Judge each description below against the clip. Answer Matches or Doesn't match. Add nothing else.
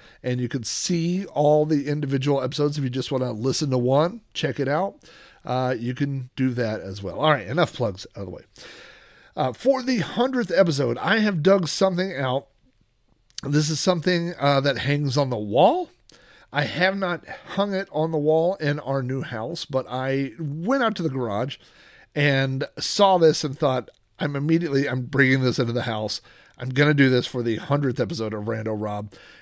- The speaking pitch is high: Doesn't match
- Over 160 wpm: Matches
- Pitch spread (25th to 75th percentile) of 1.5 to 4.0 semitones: Doesn't match